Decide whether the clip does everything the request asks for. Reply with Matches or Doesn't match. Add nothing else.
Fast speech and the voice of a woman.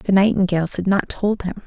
Matches